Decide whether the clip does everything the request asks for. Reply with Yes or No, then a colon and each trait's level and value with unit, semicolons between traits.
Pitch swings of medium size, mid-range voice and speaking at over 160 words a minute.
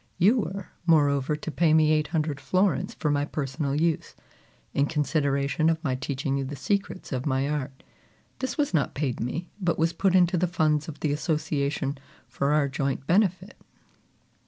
Yes: average, 3.3 semitones; medium, 150 Hz; average, 175 wpm